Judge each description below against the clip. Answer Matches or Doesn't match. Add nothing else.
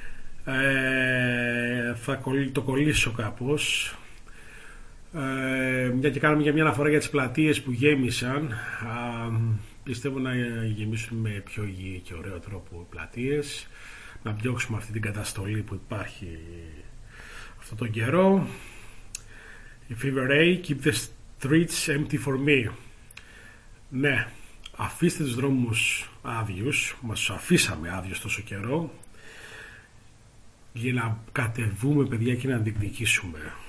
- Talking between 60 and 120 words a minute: Matches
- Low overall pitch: Matches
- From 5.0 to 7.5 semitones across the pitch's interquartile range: Doesn't match